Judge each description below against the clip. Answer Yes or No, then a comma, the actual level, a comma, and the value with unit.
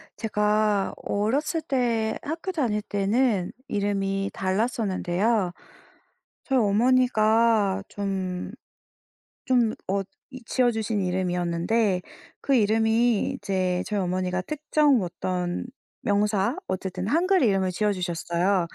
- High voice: Yes, high, 205 Hz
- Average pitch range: Yes, average, 3.8 semitones